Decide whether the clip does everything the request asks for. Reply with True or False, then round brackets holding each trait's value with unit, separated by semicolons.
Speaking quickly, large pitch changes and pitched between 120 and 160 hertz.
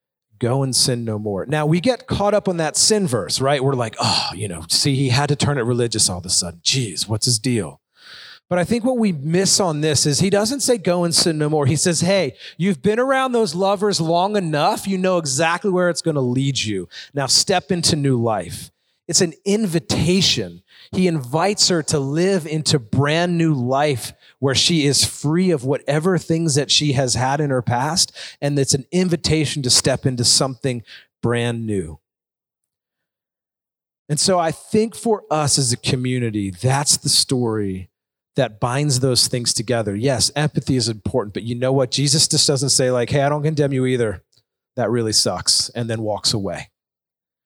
False (195 wpm; 5.7 semitones; 140 Hz)